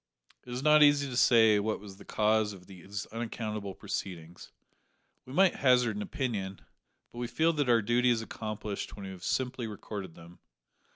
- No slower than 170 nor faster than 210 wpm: Yes, average, 180 wpm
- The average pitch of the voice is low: Yes, low, 110 Hz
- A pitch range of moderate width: Yes, average, 3.8 semitones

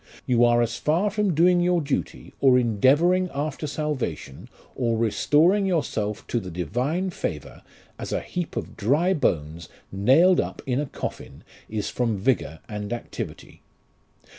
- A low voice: Yes, low, 130 Hz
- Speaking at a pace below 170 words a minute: Yes, average, 145 wpm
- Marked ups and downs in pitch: Yes, wide, 7.6 semitones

